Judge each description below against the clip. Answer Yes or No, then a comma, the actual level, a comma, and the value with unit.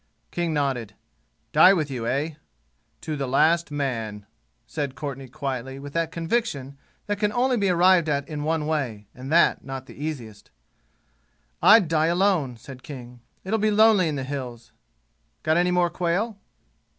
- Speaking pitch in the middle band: Yes, medium, 150 Hz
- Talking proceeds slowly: No, average, 160 wpm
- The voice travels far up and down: No, average, 4.8 semitones